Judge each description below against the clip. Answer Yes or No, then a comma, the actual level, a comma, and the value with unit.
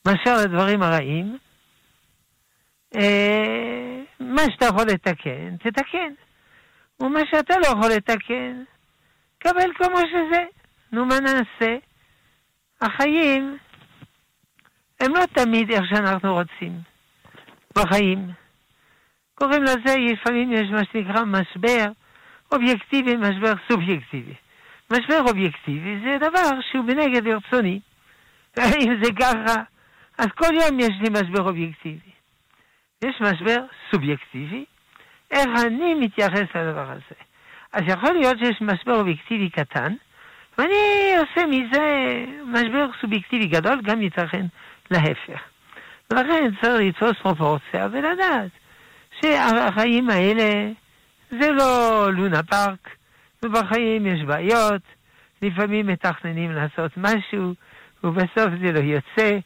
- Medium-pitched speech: No, high, 225 Hz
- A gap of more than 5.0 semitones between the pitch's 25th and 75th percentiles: Yes, wide, 5.4 semitones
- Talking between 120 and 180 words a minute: No, slow, 100 wpm